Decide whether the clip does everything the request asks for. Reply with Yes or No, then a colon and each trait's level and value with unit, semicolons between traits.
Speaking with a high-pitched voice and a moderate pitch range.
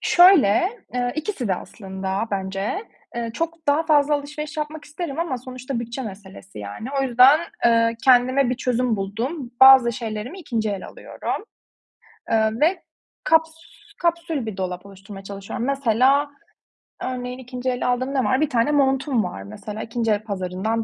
Yes: high, 245 Hz; average, 5.0 semitones